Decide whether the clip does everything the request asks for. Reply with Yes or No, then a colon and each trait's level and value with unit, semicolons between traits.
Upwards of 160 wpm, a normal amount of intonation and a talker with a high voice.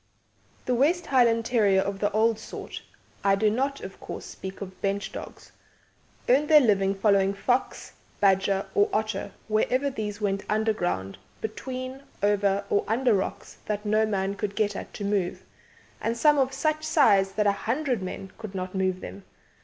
Yes: average, 170 wpm; average, 3.9 semitones; high, 210 Hz